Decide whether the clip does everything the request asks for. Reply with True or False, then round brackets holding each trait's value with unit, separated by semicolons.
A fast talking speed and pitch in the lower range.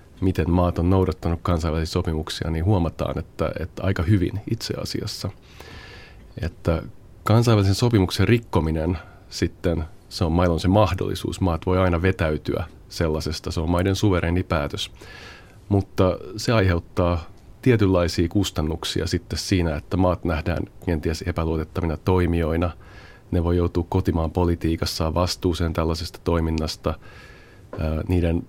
False (120 wpm; 90 Hz)